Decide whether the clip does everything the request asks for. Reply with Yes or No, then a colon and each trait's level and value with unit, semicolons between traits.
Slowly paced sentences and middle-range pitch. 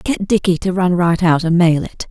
No: fast, 255 wpm; medium, 175 Hz